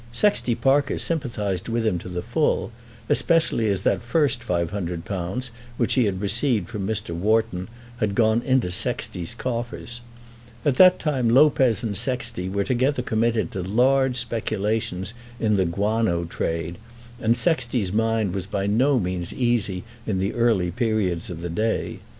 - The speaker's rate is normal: Yes, average, 150 wpm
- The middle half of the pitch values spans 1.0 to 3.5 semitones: No, average, 4.3 semitones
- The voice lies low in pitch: Yes, low, 110 Hz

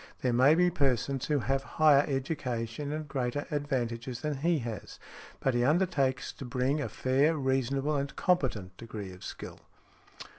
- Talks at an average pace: Yes, average, 155 wpm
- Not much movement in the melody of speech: No, average, 3.2 semitones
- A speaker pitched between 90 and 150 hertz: Yes, low, 135 Hz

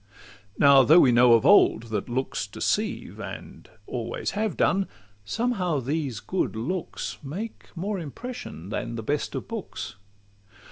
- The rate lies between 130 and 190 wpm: Yes, average, 140 wpm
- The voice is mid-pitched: Yes, medium, 145 Hz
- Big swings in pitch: Yes, wide, 8.2 semitones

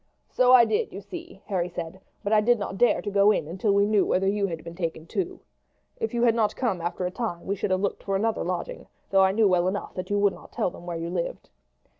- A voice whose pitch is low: No, high, 200 Hz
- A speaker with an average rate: No, fast, 265 wpm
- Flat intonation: No, average, 3.8 semitones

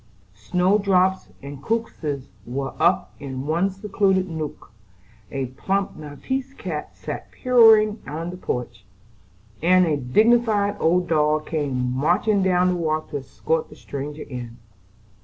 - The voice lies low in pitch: No, medium, 165 Hz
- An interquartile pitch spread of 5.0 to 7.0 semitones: Yes, wide, 5.6 semitones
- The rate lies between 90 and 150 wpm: Yes, slow, 135 wpm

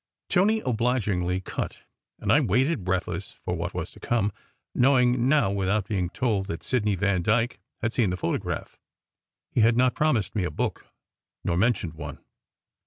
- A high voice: No, low, 110 Hz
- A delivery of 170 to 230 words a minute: No, average, 160 wpm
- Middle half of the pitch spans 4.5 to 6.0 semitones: Yes, average, 4.9 semitones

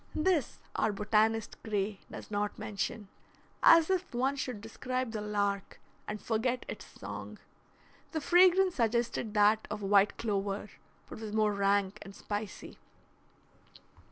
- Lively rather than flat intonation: No, average, 3.3 semitones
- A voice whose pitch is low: No, high, 215 Hz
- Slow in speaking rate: Yes, slow, 130 wpm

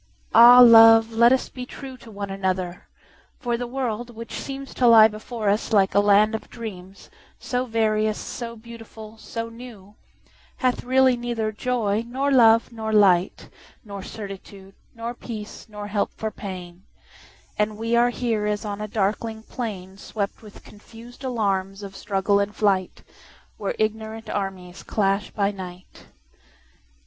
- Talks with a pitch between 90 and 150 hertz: No, high, 220 Hz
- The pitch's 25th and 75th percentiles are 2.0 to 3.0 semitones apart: Yes, narrow, 2.6 semitones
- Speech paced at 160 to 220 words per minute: No, slow, 135 wpm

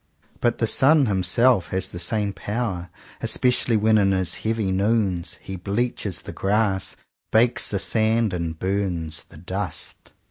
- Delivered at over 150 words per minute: No, average, 145 wpm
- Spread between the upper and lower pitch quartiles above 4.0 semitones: No, average, 3.3 semitones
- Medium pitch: No, low, 100 Hz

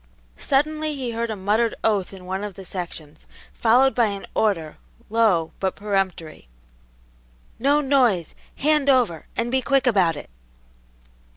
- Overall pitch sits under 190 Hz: No, high, 215 Hz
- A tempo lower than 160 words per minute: Yes, average, 145 wpm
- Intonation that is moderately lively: No, wide, 5.8 semitones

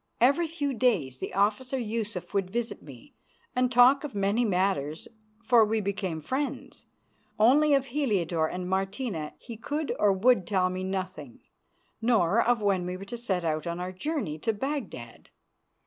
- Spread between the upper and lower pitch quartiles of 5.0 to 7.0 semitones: Yes, average, 5.3 semitones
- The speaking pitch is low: No, high, 205 Hz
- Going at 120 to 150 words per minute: No, average, 165 wpm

